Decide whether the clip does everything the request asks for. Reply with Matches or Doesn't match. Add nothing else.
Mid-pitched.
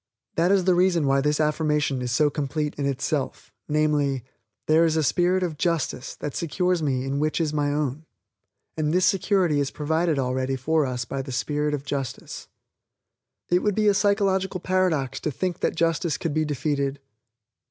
Matches